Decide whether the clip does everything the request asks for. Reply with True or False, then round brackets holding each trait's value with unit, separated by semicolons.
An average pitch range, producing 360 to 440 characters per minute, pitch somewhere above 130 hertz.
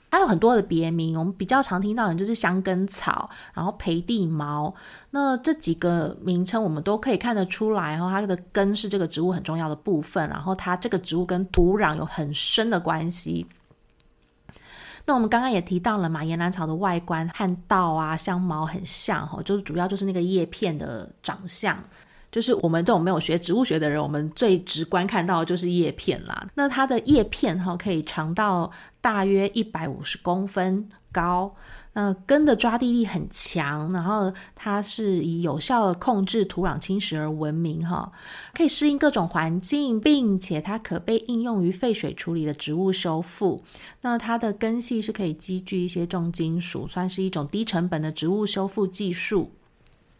False (4.1 semitones; 280 characters per minute; 185 Hz)